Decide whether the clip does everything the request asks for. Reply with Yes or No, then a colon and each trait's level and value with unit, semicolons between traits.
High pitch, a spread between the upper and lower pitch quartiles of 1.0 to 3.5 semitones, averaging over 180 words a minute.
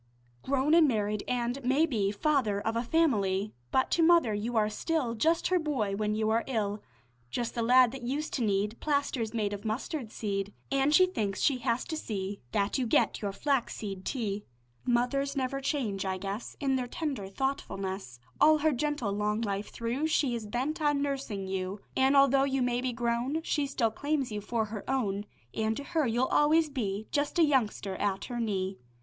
No: high, 240 Hz; average, 5.1 semitones; average, 190 wpm